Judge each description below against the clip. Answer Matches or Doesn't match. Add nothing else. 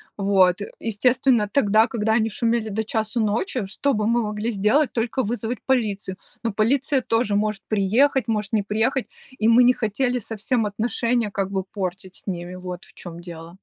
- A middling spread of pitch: Matches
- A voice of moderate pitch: Doesn't match